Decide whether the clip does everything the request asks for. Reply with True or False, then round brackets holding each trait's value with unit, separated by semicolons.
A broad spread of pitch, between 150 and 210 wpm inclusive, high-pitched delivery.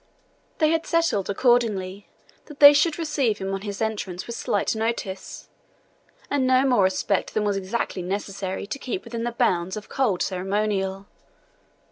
False (4.7 semitones; 155 wpm; 210 Hz)